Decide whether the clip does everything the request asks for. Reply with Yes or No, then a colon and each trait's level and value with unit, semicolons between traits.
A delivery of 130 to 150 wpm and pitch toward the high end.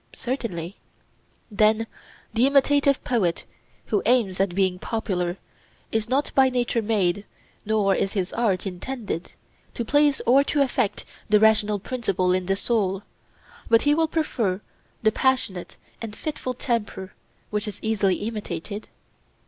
Yes: slow, 135 wpm; high, 220 Hz